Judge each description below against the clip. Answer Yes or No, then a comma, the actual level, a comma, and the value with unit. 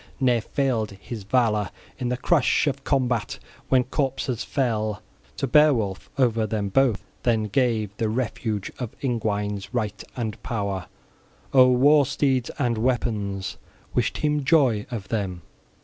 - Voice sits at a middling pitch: No, low, 120 Hz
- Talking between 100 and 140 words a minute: Yes, slow, 135 wpm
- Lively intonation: No, average, 3.8 semitones